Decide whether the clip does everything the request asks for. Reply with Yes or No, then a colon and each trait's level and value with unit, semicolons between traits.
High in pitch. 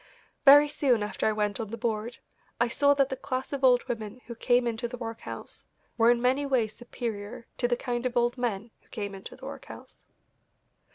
Yes: high, 240 Hz